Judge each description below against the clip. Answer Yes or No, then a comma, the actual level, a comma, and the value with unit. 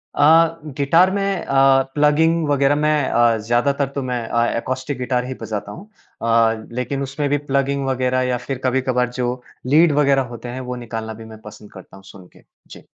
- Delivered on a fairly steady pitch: No, average, 3.3 semitones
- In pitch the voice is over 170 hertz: No, low, 130 Hz